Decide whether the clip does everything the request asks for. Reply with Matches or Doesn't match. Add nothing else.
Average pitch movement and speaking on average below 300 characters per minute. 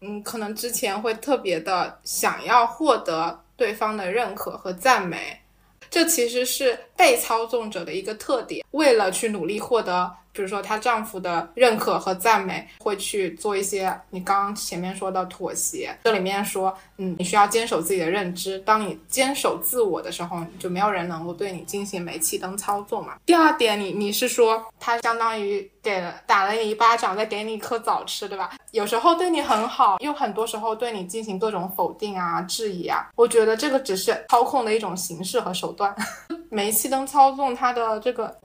Matches